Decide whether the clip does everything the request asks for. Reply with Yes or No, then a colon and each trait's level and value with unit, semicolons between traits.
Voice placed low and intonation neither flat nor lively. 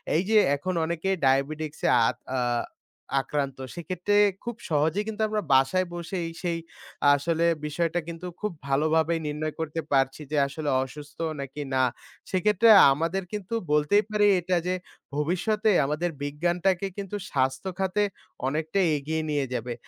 No: medium, 165 Hz; average, 4.2 semitones